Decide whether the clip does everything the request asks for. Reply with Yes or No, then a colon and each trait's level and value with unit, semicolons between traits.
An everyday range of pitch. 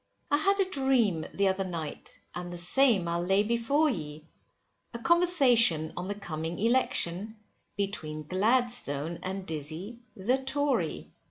No: wide, 6.9 semitones